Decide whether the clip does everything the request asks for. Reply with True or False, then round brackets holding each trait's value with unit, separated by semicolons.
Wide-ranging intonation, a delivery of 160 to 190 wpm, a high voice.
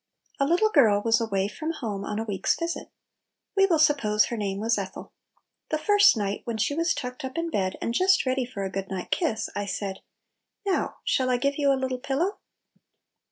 False (7.1 semitones; 205 wpm; 250 Hz)